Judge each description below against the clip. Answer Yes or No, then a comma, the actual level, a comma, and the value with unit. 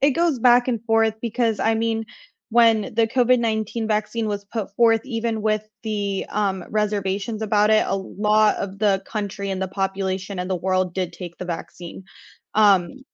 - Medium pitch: No, high, 215 Hz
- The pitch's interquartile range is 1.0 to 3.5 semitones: Yes, average, 2.7 semitones